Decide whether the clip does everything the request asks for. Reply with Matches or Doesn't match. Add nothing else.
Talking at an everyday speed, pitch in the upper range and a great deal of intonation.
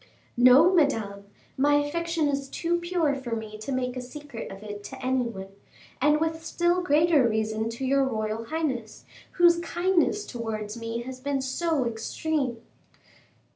Matches